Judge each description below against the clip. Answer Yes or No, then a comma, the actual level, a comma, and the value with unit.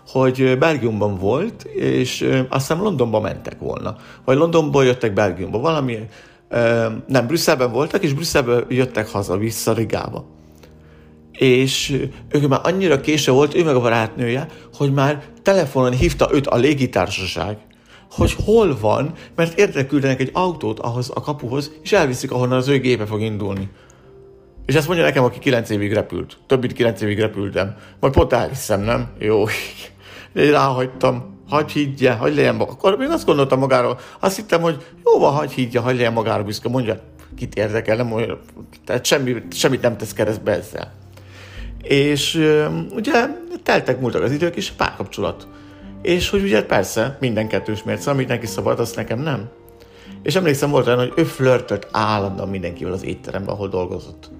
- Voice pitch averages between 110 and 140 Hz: Yes, low, 125 Hz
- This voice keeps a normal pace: No, fast, 160 wpm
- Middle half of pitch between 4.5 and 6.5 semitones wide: Yes, wide, 5.5 semitones